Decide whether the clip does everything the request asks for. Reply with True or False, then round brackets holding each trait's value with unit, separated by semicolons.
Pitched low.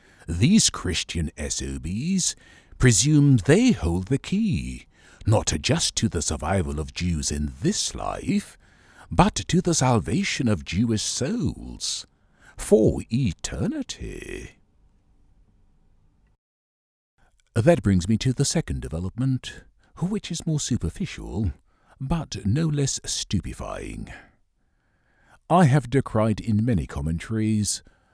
True (110 Hz)